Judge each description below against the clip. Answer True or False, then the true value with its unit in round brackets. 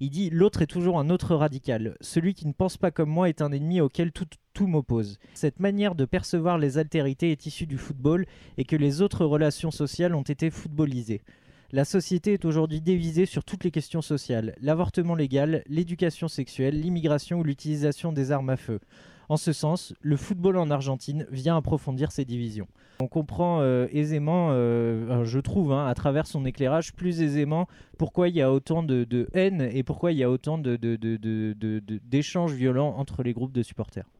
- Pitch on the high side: False (150 Hz)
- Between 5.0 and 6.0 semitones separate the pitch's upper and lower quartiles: False (4.2 semitones)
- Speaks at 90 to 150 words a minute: False (200 wpm)